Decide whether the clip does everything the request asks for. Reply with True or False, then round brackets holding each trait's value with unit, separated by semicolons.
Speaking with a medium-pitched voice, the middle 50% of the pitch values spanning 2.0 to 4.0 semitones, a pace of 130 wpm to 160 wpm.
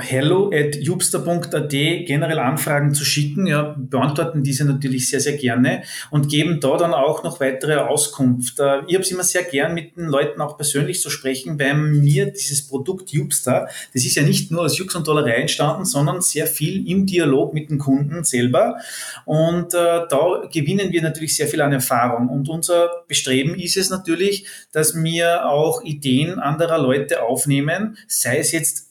False (150 Hz; 3.4 semitones; 180 wpm)